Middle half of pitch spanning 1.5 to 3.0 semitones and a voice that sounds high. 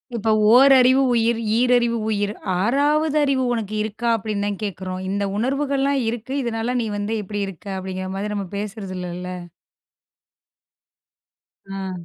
No: average, 4.1 semitones; high, 220 Hz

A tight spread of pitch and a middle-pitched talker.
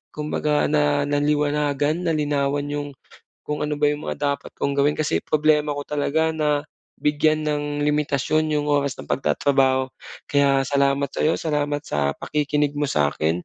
Yes: narrow, 1.0 semitones; medium, 145 Hz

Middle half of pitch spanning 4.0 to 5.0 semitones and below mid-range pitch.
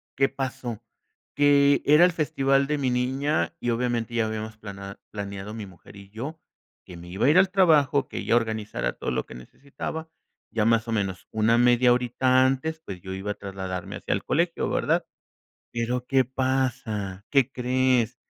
Yes: average, 4.5 semitones; low, 120 Hz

